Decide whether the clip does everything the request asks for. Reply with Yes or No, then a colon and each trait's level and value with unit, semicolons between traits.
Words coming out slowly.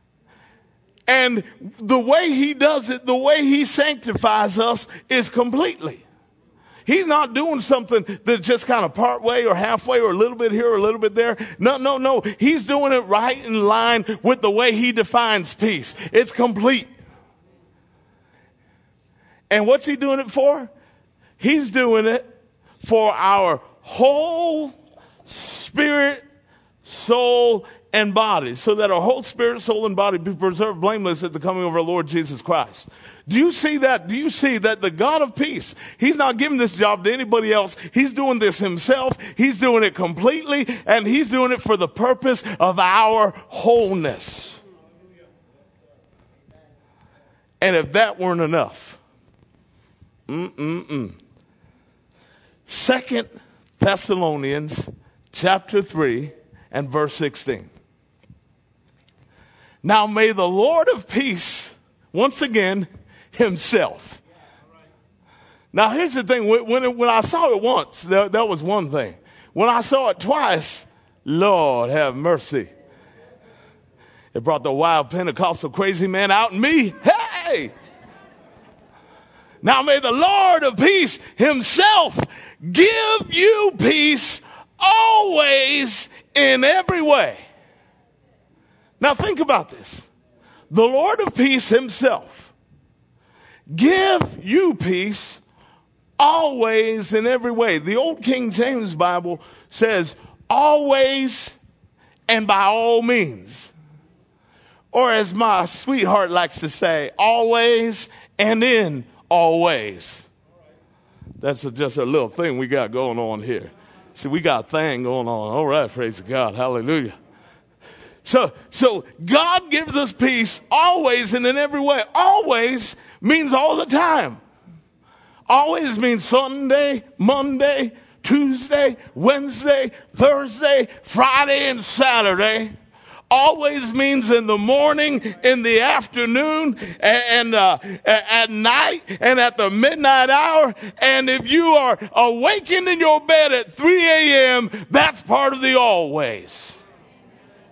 Yes: slow, 130 wpm